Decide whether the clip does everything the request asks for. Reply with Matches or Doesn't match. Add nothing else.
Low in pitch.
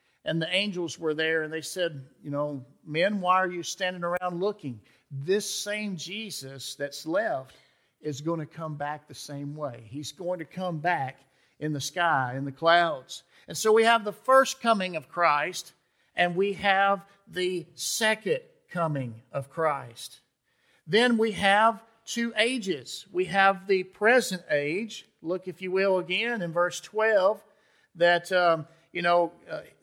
Doesn't match